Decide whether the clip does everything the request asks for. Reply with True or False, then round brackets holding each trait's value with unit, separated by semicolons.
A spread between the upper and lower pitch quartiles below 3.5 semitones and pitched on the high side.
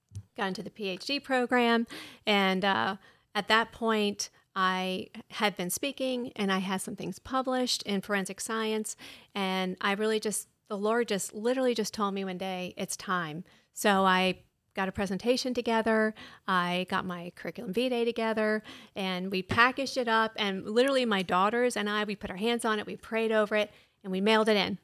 True (3.1 semitones; 210 Hz)